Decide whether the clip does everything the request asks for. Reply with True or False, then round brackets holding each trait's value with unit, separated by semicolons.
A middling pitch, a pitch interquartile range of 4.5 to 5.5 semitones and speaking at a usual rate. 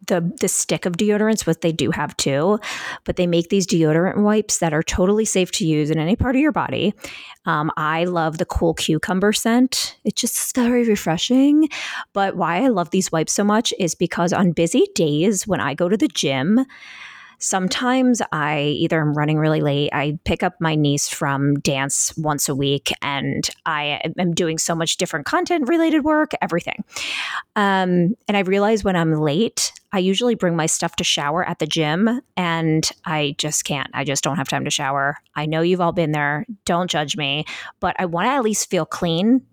True (175 Hz; 5.0 semitones; 195 wpm)